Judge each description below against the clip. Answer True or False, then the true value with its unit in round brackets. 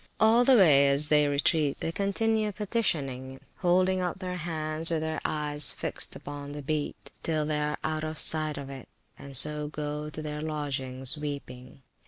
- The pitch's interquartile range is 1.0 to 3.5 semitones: True (2.5 semitones)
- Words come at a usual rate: True (175 wpm)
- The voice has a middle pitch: True (150 Hz)